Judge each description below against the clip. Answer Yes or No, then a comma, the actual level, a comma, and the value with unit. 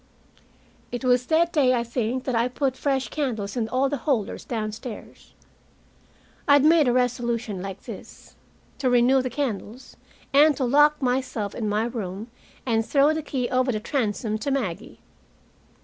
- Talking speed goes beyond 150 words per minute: Yes, average, 165 wpm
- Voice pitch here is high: Yes, very high, 250 Hz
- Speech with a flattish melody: No, average, 3.6 semitones